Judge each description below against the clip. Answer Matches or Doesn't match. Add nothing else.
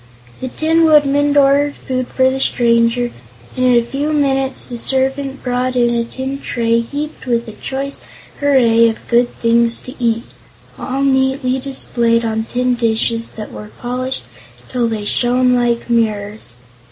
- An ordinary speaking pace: Matches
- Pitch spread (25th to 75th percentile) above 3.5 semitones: Doesn't match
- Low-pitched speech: Doesn't match